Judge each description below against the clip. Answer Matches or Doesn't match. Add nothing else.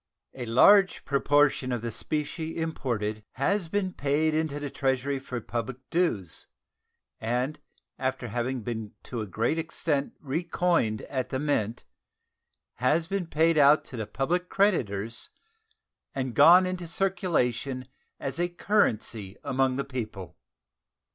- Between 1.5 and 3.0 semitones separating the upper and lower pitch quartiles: Doesn't match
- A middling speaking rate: Doesn't match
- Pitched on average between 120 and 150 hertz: Matches